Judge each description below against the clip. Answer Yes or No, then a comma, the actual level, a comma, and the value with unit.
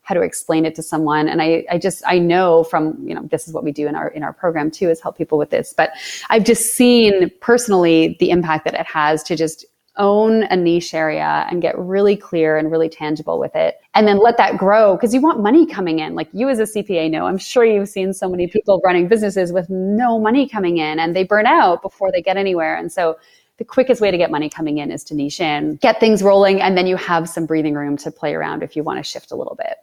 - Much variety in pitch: No, average, 4.4 semitones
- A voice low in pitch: No, medium, 180 Hz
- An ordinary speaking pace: No, fast, 260 wpm